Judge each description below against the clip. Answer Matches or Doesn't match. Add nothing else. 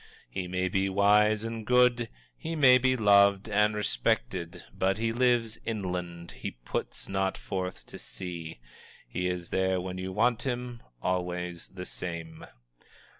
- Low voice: Matches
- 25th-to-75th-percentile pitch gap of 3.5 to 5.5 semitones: Matches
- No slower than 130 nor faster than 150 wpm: Matches